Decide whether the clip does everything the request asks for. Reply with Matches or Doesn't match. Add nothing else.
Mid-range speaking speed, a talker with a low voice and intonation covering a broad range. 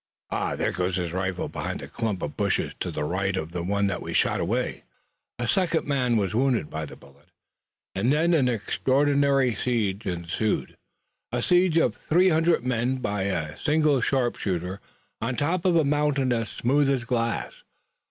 Matches